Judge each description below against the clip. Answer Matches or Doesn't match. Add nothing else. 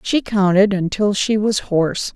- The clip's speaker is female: Matches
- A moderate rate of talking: Matches